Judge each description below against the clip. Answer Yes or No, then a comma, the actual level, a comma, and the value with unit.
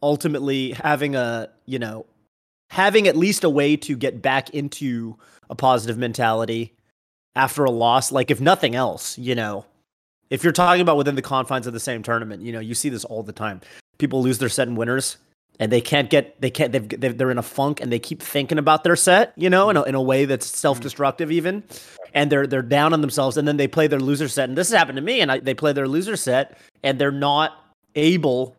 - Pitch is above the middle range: No, low, 135 Hz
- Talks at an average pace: No, fast, 230 wpm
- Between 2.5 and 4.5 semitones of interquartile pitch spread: Yes, average, 3.4 semitones